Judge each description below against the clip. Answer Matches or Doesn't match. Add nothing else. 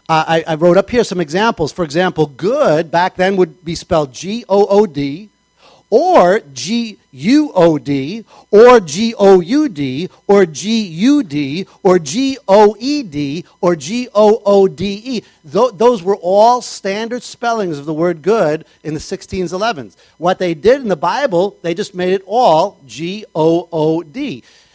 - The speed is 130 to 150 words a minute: Doesn't match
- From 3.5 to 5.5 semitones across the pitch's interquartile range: Matches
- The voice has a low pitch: Doesn't match